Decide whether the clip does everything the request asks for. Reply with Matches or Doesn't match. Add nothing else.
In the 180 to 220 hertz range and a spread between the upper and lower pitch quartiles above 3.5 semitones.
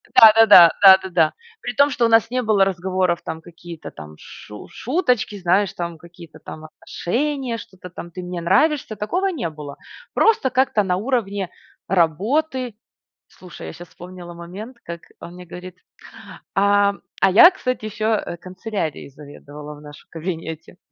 Matches